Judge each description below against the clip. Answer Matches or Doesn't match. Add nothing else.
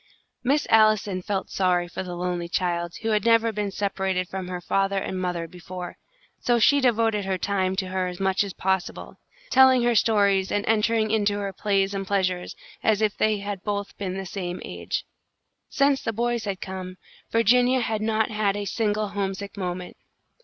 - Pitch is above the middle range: Matches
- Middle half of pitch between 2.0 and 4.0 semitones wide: Matches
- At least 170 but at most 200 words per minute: Matches